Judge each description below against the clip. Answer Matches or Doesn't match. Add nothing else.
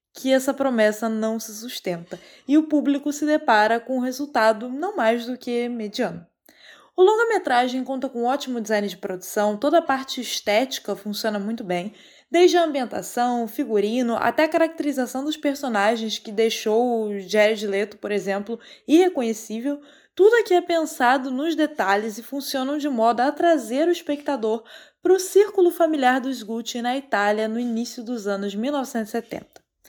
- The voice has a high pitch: Matches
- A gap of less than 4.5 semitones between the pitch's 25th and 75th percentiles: Doesn't match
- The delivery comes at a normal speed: Matches